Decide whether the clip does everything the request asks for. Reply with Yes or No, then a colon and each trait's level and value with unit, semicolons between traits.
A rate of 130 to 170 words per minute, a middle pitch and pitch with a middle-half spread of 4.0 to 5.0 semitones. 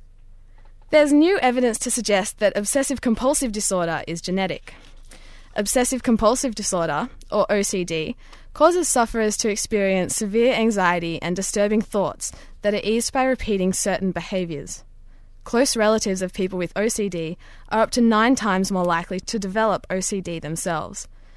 No: average, 140 wpm; high, 205 Hz; average, 4.7 semitones